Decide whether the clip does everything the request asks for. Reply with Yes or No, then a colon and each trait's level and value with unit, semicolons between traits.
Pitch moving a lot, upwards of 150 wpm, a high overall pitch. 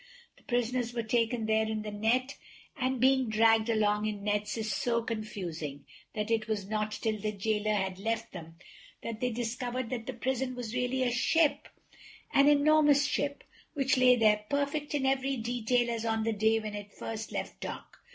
No: average, 3.0 semitones; average, 180 wpm; high, 230 Hz